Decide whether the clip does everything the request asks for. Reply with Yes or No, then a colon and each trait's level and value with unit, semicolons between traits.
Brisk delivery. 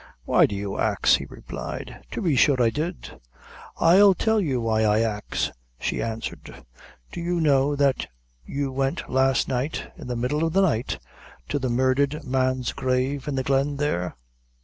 No: average, 170 wpm